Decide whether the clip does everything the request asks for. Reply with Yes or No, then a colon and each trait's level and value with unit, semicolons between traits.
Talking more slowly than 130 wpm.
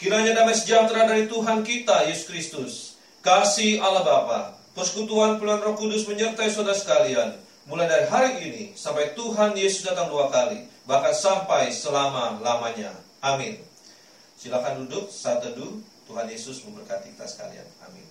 No: fast, 140 wpm